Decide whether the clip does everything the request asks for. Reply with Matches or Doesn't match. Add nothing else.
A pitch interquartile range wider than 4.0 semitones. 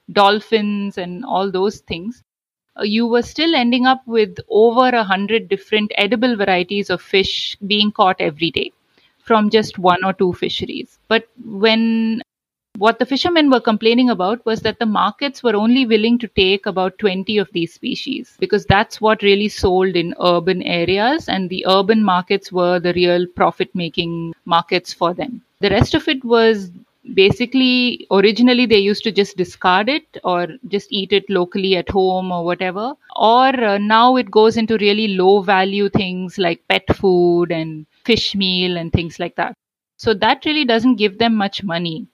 Doesn't match